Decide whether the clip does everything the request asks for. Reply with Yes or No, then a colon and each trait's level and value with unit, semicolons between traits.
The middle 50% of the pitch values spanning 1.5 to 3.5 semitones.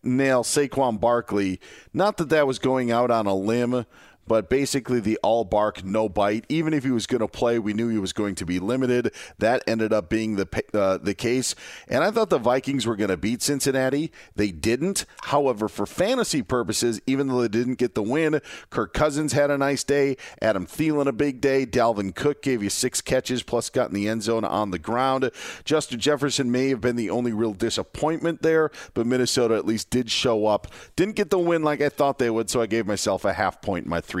No: average, 3.9 semitones